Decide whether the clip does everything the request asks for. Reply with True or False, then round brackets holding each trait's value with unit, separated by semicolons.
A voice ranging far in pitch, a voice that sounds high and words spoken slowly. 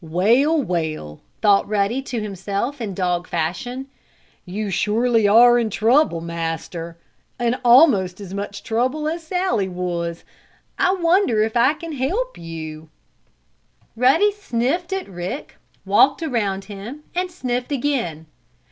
True (7.3 semitones; 225 Hz; 125 wpm)